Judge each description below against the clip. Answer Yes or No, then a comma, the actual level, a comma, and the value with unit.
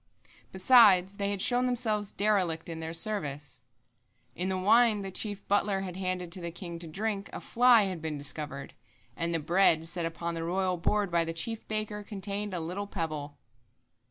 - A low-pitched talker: No, medium, 185 Hz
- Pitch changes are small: No, average, 3.8 semitones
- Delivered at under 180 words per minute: No, average, 185 wpm